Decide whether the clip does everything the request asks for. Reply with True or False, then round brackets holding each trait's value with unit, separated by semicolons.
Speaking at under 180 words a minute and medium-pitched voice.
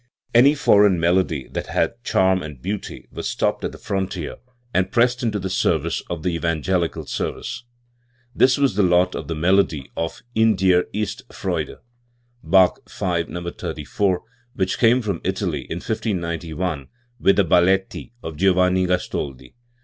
False (150 wpm; 90 Hz)